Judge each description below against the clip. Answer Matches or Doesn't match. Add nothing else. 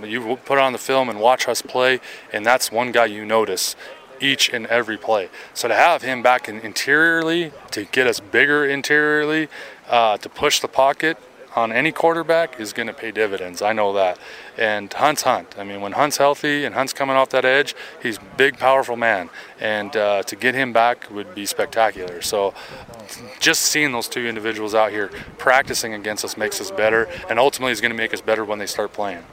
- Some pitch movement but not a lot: Matches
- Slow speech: Doesn't match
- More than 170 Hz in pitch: Doesn't match